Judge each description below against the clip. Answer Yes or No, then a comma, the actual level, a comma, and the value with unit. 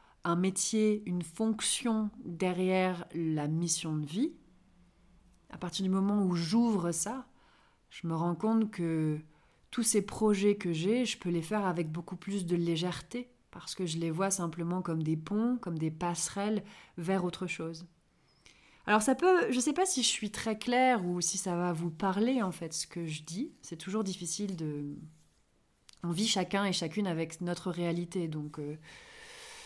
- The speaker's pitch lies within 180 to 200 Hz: Yes, medium, 185 Hz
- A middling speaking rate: Yes, average, 180 wpm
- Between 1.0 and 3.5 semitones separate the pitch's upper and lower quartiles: No, average, 4.1 semitones